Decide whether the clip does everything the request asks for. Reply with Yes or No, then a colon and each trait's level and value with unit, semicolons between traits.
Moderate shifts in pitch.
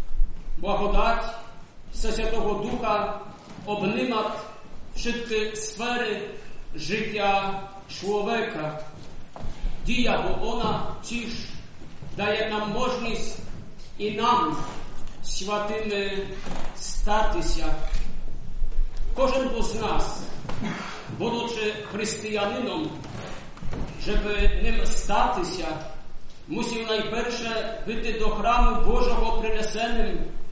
No: narrow, 1.9 semitones